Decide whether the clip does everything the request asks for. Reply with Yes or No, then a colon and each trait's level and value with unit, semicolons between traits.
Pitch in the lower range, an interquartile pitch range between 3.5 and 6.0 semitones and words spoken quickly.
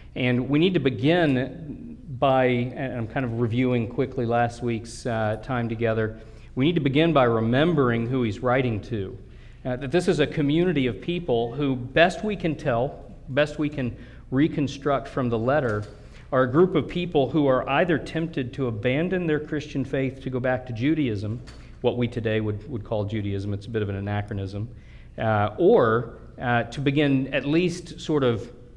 No: low, 130 Hz; average, 4.1 semitones; average, 185 wpm